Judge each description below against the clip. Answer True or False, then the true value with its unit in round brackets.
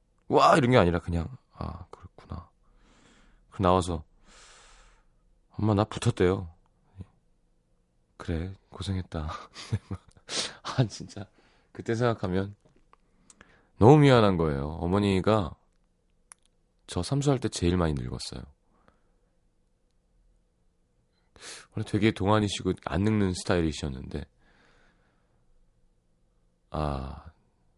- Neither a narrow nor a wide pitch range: False (5.9 semitones)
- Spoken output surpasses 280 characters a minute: False (180 characters per minute)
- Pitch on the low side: True (90 Hz)